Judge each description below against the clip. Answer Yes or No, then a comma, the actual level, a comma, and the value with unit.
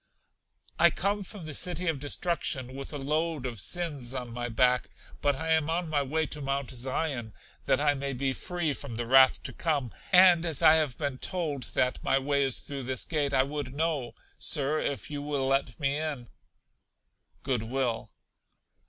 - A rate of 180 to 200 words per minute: Yes, average, 190 wpm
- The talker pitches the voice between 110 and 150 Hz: Yes, medium, 140 Hz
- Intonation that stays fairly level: No, average, 3.3 semitones